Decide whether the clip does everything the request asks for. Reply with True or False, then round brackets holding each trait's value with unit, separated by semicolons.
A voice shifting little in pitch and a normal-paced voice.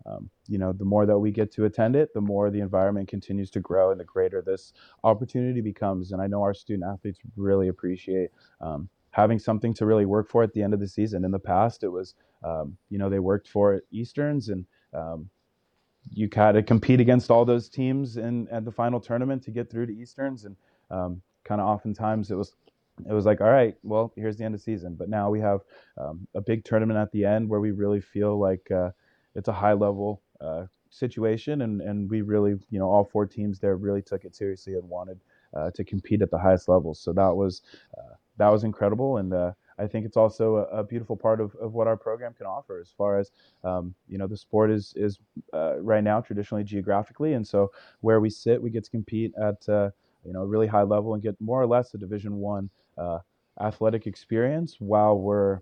False (2.2 semitones; 225 wpm)